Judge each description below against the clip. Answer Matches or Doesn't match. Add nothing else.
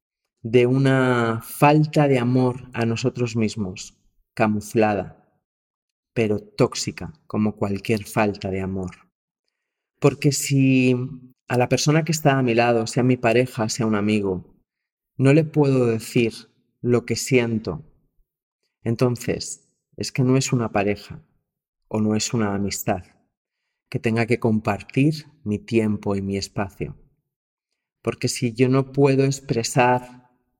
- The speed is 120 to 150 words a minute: Matches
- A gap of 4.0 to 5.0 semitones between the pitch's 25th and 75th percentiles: Doesn't match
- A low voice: Matches